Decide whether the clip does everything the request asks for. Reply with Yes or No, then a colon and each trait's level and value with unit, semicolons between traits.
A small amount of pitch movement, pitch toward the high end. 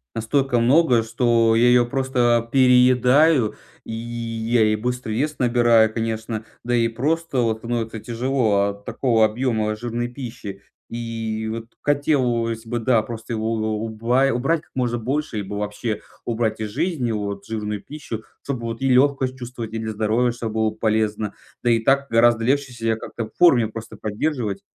No: narrow, 2.2 semitones; low, 115 Hz